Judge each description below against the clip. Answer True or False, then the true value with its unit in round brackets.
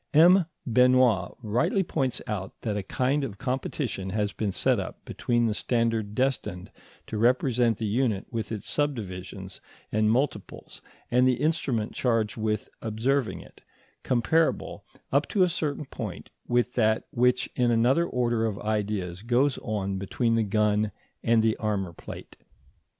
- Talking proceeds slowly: False (150 wpm)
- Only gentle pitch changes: False (3.3 semitones)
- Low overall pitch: True (115 Hz)